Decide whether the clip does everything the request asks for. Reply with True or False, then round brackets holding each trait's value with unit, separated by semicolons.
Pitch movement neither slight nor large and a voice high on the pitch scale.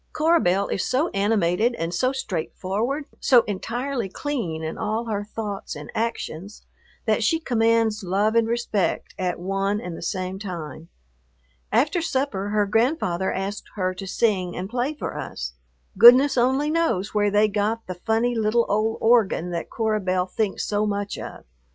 True (4.0 semitones; 210 Hz)